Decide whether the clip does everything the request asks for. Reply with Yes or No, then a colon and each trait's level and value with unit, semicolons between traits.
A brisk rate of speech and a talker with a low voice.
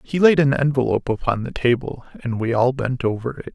Yes: fast, 220 wpm; low, 125 Hz